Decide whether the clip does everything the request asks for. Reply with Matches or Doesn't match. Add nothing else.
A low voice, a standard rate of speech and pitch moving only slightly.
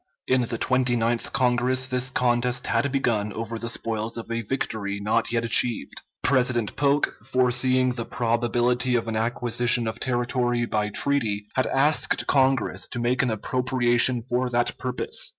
Matches